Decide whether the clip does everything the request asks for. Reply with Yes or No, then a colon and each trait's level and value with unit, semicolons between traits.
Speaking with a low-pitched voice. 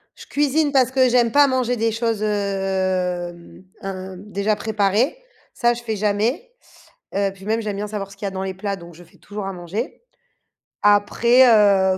No: high, 205 Hz